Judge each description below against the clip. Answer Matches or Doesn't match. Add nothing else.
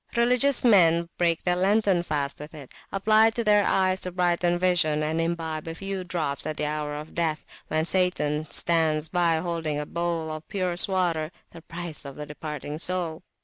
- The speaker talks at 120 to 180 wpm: Doesn't match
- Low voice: Doesn't match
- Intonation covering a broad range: Doesn't match